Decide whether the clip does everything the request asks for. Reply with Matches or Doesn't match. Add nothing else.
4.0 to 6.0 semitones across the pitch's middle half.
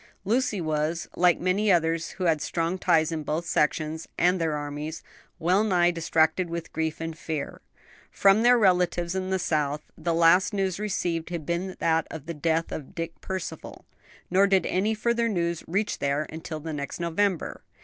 Doesn't match